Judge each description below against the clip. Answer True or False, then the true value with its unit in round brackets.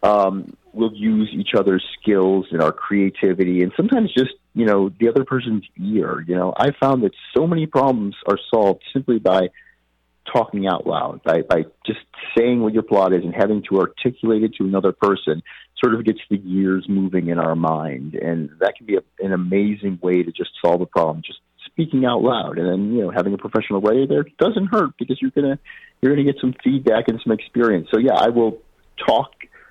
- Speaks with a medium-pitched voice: False (105 Hz)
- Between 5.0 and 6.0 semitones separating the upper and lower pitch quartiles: True (5.5 semitones)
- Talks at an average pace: False (210 wpm)